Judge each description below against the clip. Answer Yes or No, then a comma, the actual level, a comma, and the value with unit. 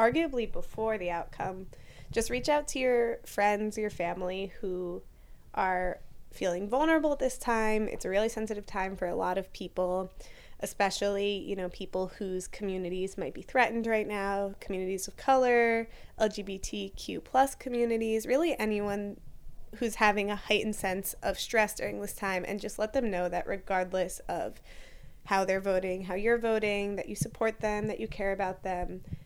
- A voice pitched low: No, high, 200 Hz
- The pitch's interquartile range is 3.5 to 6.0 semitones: No, average, 3.1 semitones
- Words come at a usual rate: Yes, average, 165 wpm